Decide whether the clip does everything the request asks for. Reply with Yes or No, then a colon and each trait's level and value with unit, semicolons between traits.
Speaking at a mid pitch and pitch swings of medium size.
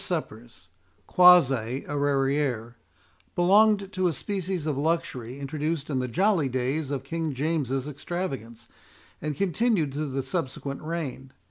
Yes: medium, 145 Hz; average, 4.3 semitones